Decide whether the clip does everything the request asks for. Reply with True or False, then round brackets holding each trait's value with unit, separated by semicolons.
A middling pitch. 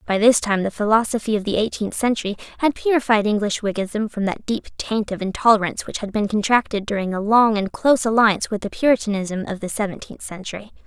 False (210 Hz)